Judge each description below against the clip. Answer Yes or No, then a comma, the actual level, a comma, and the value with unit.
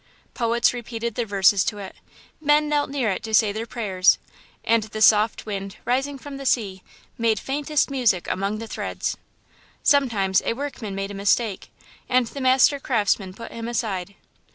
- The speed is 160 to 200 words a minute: Yes, average, 170 wpm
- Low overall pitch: No, high, 225 Hz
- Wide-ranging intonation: No, average, 4.3 semitones